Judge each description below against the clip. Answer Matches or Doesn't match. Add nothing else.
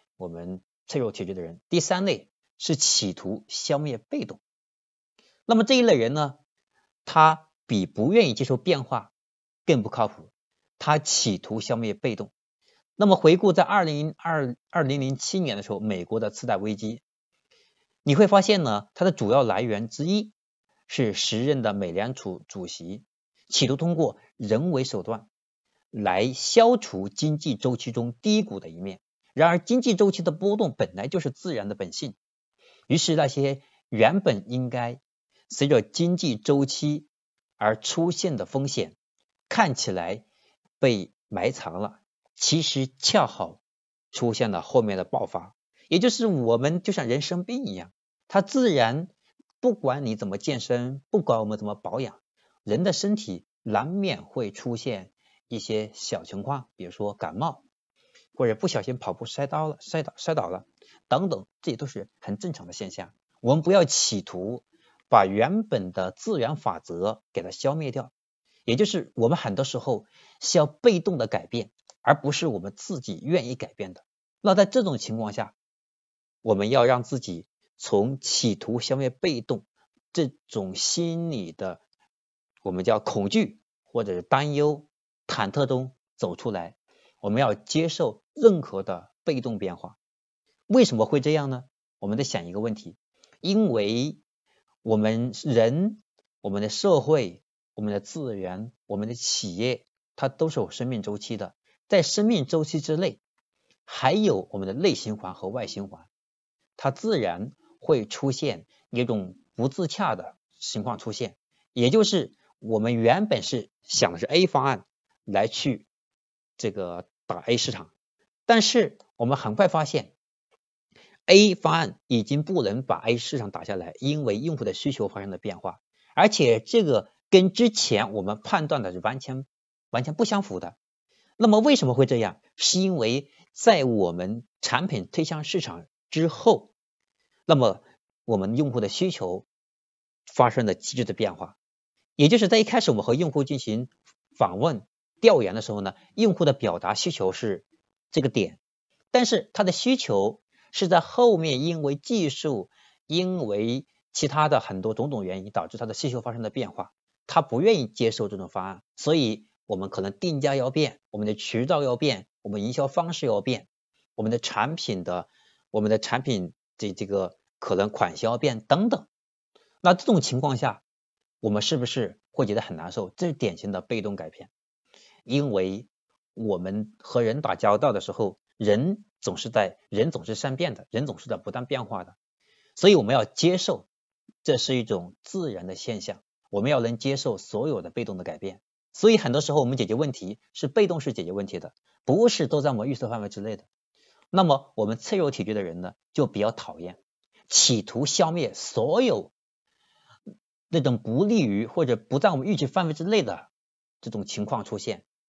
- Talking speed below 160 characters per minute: Doesn't match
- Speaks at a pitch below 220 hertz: Matches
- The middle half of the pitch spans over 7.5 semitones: Matches